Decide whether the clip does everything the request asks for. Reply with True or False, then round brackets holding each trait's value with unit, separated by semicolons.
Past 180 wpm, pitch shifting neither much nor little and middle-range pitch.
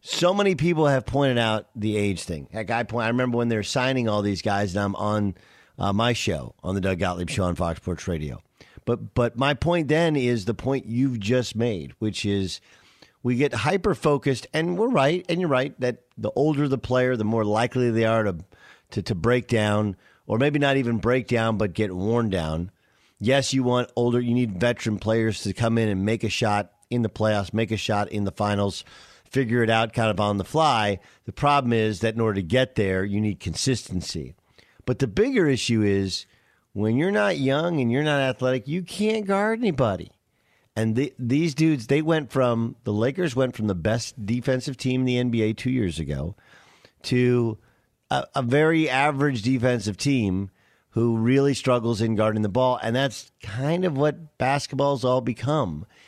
False (200 wpm; 4.4 semitones; 120 Hz)